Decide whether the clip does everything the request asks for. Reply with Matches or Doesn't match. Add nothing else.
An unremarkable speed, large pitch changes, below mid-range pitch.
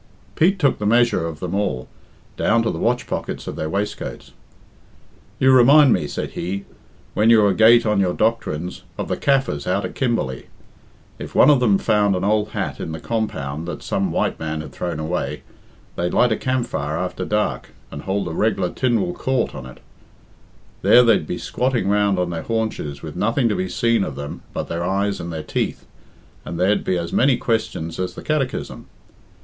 Matches